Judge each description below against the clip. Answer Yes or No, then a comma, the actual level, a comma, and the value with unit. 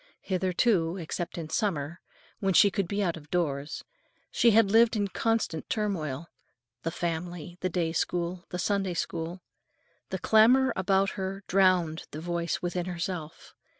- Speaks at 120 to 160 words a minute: Yes, average, 150 wpm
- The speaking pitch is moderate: Yes, medium, 180 Hz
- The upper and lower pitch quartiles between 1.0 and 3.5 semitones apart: Yes, average, 2.8 semitones